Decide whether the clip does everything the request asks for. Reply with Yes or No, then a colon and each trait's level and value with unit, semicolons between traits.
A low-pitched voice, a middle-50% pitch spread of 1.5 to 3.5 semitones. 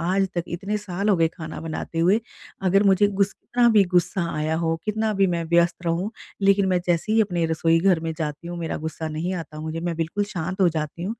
No: medium, 175 Hz; average, 3.1 semitones